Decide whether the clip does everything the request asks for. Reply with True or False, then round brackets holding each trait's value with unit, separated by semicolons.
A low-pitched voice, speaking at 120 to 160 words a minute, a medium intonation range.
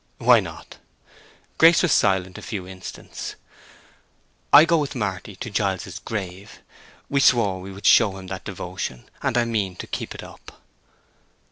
True (100 Hz; 155 wpm; 3.9 semitones)